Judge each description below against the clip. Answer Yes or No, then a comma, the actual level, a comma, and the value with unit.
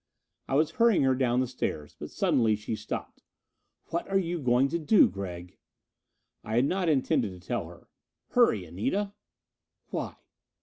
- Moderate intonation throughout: No, wide, 8.1 semitones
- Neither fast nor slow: Yes, average, 160 wpm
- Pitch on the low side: Yes, low, 130 Hz